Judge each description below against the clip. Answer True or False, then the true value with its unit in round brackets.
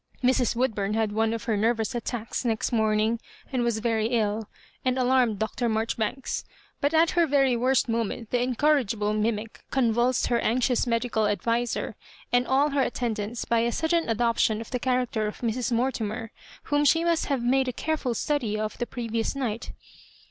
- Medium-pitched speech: False (235 Hz)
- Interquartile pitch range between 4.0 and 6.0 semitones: False (2.7 semitones)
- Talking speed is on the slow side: False (175 wpm)